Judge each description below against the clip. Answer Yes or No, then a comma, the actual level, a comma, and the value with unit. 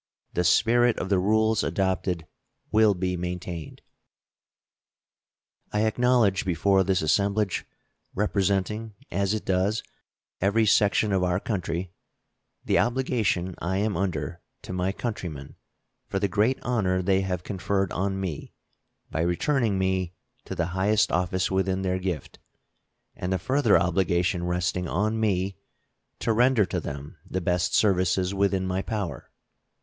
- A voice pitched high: No, very low, 95 Hz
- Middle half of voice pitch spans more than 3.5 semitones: No, narrow, 2.6 semitones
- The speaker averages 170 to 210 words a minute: No, slow, 135 wpm